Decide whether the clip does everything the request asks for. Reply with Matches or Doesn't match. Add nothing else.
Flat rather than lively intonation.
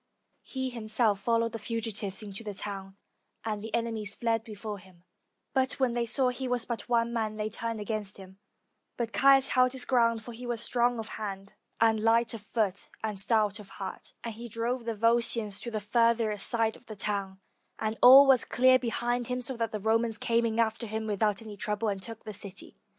Matches